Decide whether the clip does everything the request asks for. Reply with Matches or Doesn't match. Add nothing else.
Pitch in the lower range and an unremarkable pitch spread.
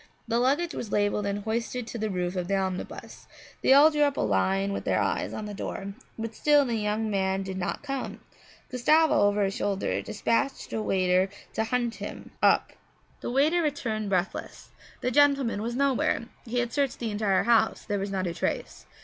Doesn't match